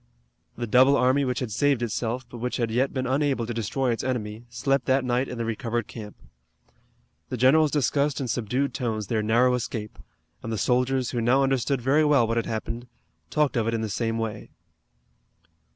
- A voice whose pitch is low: Yes, low, 125 Hz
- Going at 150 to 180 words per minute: No, average, 195 wpm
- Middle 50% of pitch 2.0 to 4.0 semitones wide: Yes, average, 2.7 semitones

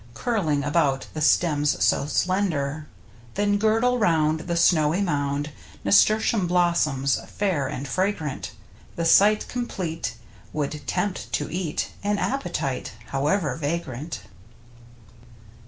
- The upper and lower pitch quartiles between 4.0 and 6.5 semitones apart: Yes, wide, 5.5 semitones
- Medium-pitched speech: Yes, medium, 165 Hz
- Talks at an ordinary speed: No, slow, 110 wpm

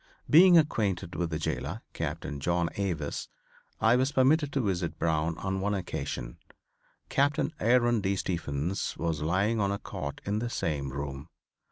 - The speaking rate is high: No, average, 155 wpm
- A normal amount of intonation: No, wide, 6.6 semitones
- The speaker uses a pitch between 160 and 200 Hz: No, very low, 95 Hz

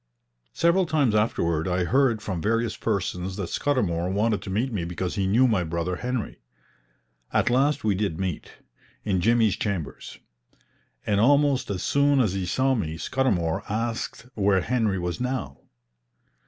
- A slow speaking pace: No, average, 155 wpm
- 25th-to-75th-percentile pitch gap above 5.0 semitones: Yes, wide, 5.6 semitones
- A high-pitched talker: No, low, 105 Hz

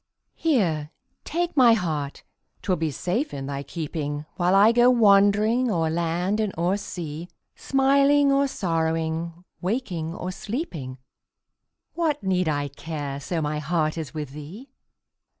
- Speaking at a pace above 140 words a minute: No, slow, 135 wpm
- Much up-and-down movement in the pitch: Yes, wide, 6.6 semitones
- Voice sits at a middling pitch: Yes, medium, 175 Hz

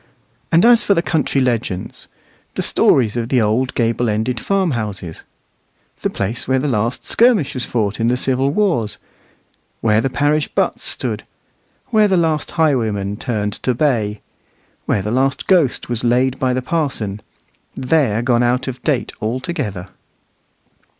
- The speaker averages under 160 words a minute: Yes, average, 150 wpm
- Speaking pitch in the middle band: No, low, 125 Hz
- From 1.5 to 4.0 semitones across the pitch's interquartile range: No, average, 4.9 semitones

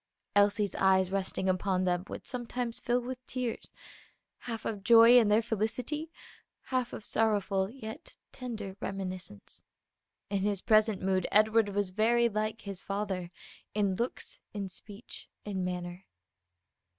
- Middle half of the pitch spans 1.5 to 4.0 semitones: Yes, average, 3.2 semitones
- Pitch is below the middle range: No, high, 205 Hz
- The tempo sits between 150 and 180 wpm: No, slow, 135 wpm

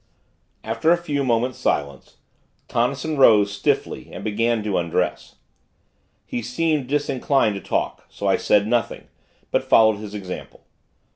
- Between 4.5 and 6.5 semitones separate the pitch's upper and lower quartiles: Yes, average, 4.8 semitones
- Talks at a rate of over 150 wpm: No, slow, 135 wpm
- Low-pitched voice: Yes, low, 115 Hz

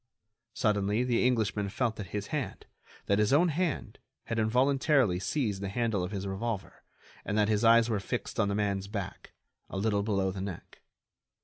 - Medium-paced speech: Yes, average, 175 wpm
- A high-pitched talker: No, low, 105 Hz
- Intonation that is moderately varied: Yes, average, 3.0 semitones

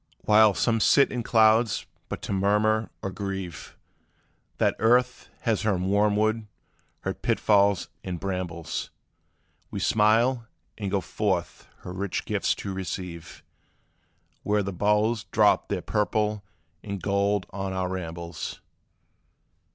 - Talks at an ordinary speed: No, slow, 120 wpm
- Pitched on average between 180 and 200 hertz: No, low, 100 Hz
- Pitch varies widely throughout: No, narrow, 2.5 semitones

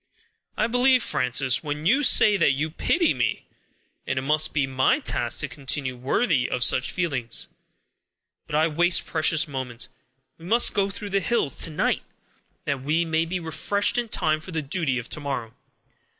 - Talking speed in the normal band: Yes, average, 185 wpm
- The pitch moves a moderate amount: No, wide, 5.8 semitones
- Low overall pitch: No, medium, 155 Hz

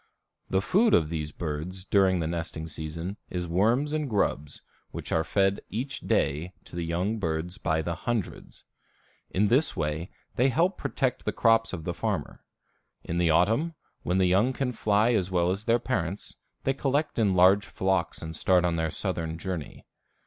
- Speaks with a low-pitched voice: Yes, very low, 95 Hz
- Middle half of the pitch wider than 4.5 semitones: Yes, wide, 5.5 semitones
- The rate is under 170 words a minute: No, average, 180 wpm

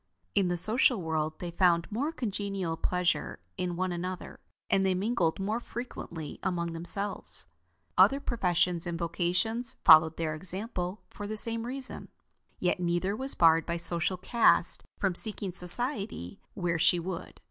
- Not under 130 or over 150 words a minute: Yes, average, 145 wpm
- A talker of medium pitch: Yes, medium, 180 Hz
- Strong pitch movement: No, average, 3.7 semitones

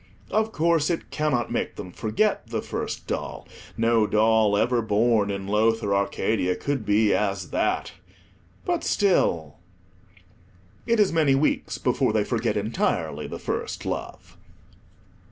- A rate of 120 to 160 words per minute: Yes, slow, 135 wpm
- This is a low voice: Yes, low, 110 Hz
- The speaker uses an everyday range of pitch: No, wide, 5.7 semitones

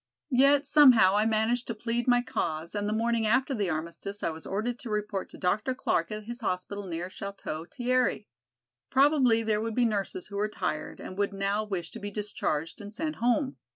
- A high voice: Yes, high, 215 Hz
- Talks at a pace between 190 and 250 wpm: Yes, average, 200 wpm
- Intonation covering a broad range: No, average, 3.7 semitones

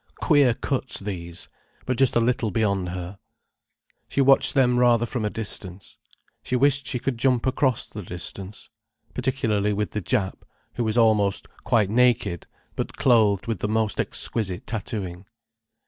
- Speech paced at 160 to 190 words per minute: No, average, 150 wpm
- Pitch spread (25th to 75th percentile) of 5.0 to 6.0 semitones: No, average, 4.0 semitones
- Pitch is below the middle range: Yes, low, 110 Hz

